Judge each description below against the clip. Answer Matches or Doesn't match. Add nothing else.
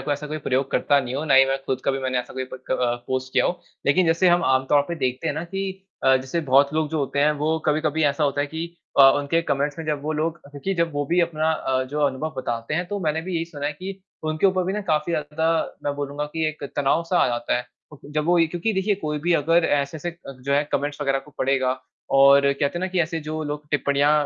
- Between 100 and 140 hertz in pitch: Doesn't match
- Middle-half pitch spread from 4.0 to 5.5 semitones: Doesn't match